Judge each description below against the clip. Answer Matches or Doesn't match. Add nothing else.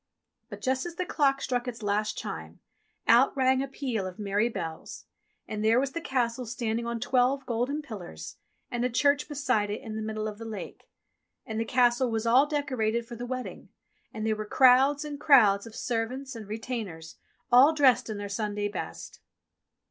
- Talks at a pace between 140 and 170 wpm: Doesn't match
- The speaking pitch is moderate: Doesn't match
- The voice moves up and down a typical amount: Matches